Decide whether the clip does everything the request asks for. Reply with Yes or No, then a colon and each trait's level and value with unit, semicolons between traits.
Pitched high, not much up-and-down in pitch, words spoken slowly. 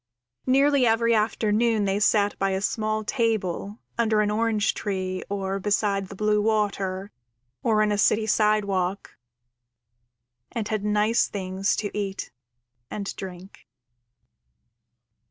Yes: high, 210 Hz; narrow, 1.8 semitones; slow, 120 wpm